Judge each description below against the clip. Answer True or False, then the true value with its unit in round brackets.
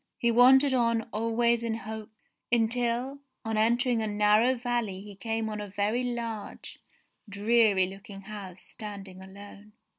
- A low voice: False (220 Hz)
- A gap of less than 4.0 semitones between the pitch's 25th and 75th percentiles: True (2.6 semitones)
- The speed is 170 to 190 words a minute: False (140 wpm)